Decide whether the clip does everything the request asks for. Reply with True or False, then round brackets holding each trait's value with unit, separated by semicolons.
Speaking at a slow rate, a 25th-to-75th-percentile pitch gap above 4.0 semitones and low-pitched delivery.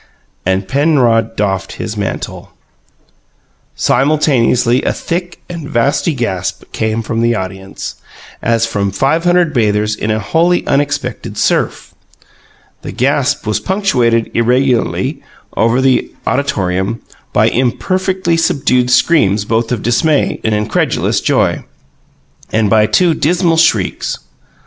True (115 wpm; 5.5 semitones; 125 Hz)